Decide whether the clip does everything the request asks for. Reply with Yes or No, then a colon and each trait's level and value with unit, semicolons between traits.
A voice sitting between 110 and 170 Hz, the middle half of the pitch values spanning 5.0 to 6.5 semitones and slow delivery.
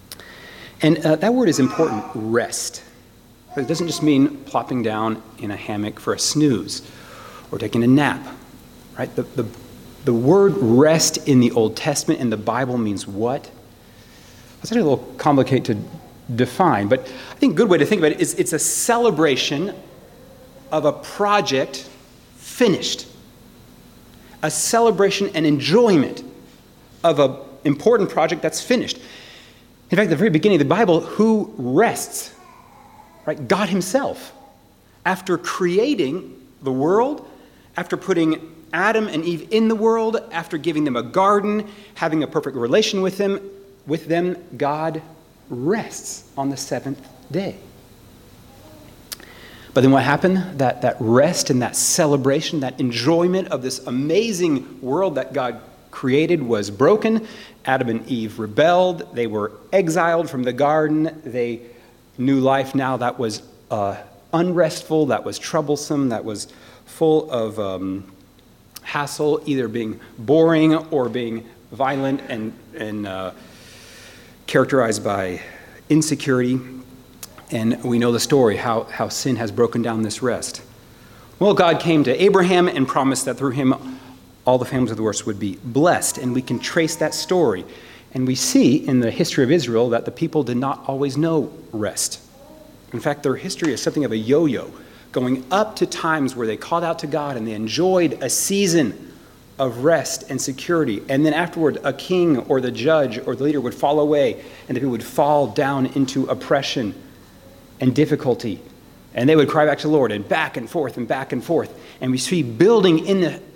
No: medium, 140 Hz; wide, 5.4 semitones; average, 160 wpm